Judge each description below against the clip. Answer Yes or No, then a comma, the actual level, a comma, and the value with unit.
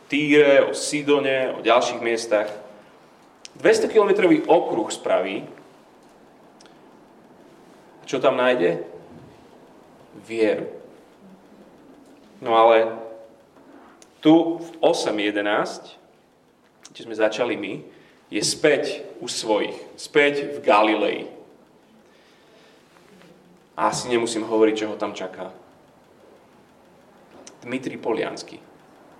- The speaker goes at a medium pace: No, slow, 85 wpm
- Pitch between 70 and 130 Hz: Yes, low, 125 Hz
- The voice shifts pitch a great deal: Yes, wide, 7.5 semitones